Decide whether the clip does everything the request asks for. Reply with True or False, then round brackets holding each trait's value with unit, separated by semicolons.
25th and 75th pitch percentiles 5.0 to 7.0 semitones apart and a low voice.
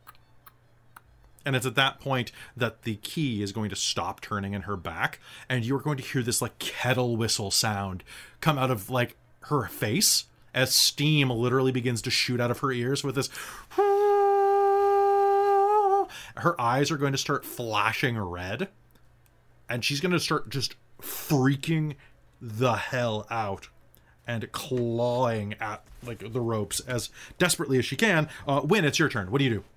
False (4.0 semitones; 125 Hz)